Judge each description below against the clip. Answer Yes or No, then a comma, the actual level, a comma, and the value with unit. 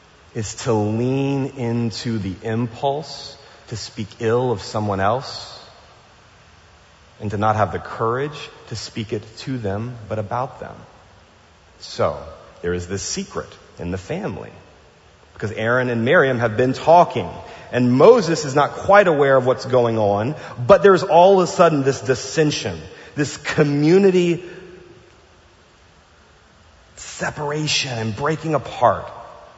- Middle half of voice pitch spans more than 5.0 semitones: Yes, wide, 5.5 semitones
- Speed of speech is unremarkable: No, slow, 130 wpm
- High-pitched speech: No, low, 120 Hz